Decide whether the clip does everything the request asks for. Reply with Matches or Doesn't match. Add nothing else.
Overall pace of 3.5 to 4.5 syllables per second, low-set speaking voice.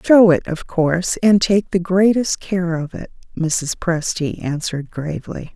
Doesn't match